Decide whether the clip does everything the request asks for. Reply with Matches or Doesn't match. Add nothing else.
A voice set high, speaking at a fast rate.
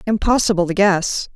Doesn't match